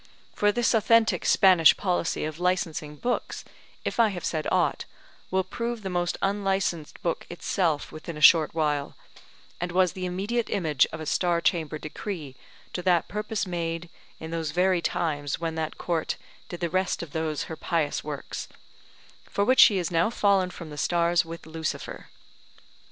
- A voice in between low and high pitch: Yes, medium, 170 Hz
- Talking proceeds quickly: No, average, 170 wpm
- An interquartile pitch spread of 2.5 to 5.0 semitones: Yes, average, 3.1 semitones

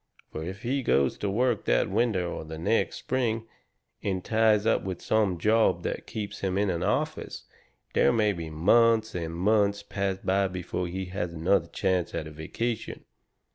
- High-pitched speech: No, very low, 95 Hz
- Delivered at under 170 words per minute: No, average, 175 wpm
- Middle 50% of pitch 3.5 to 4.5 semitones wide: Yes, average, 3.9 semitones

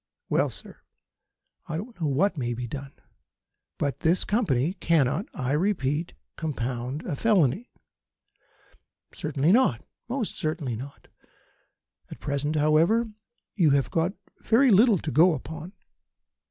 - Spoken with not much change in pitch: No, wide, 5.6 semitones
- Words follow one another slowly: Yes, slow, 125 wpm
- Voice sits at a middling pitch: Yes, medium, 155 Hz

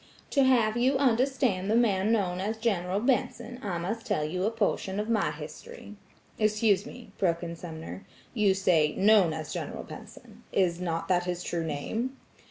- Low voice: No, high, 195 Hz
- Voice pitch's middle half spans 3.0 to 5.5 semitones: Yes, average, 4.6 semitones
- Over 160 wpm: Yes, average, 175 wpm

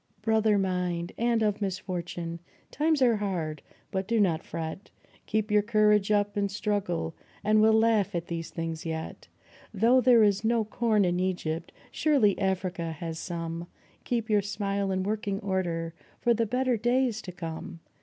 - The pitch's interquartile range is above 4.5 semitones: No, average, 4.1 semitones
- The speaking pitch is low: No, high, 200 Hz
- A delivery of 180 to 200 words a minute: No, average, 160 wpm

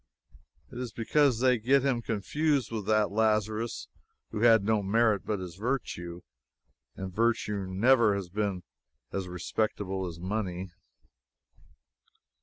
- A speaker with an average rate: No, slow, 125 wpm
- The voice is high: No, low, 110 Hz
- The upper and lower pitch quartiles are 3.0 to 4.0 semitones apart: Yes, average, 3.6 semitones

